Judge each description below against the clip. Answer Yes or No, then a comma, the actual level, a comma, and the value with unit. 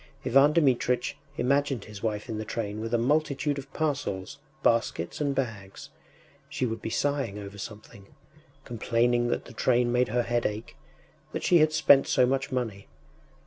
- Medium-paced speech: Yes, average, 165 wpm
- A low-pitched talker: Yes, low, 120 Hz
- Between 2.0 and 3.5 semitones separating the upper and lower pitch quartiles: No, average, 4.0 semitones